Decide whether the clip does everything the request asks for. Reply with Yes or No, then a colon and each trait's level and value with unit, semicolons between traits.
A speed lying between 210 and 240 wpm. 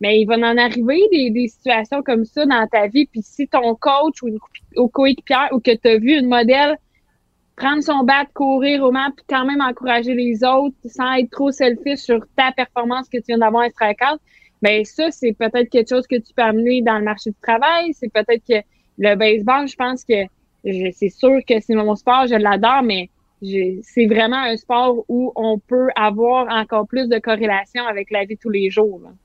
Yes: average, 215 wpm